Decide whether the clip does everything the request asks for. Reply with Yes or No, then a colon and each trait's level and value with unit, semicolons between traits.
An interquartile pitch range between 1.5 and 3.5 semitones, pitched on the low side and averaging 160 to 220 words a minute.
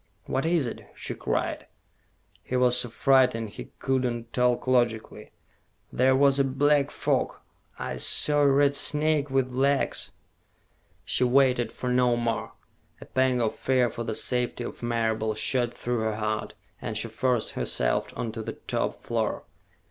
Yes: narrow, 2.5 semitones; low, 125 Hz; average, 165 wpm